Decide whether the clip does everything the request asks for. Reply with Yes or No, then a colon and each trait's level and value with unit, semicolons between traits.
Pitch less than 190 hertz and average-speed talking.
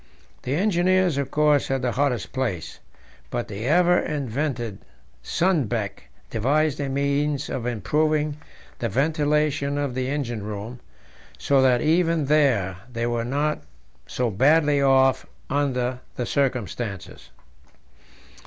No: low, 135 Hz; slow, 120 wpm